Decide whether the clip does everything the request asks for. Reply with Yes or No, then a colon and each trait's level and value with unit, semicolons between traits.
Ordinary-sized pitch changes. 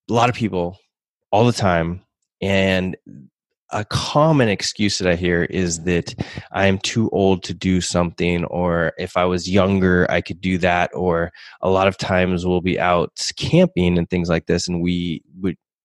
No: narrow, 1.9 semitones